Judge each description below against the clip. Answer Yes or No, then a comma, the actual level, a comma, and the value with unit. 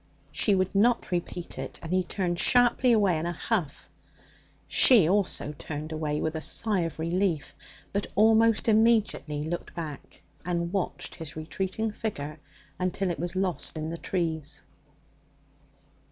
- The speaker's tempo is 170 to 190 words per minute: No, average, 145 wpm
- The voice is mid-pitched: Yes, medium, 175 Hz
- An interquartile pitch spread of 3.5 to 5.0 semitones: Yes, average, 4.3 semitones